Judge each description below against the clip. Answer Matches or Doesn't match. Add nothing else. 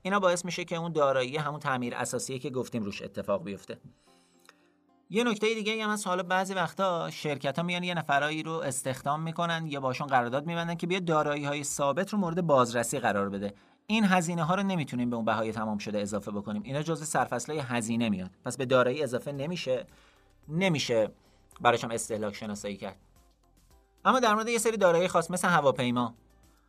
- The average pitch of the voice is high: Doesn't match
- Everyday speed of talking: Doesn't match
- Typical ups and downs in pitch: Doesn't match